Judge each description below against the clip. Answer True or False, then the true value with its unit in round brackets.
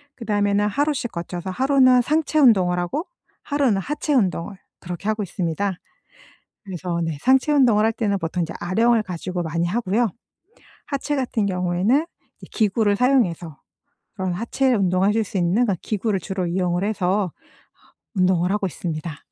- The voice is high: True (200 Hz)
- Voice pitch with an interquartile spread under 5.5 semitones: True (5.1 semitones)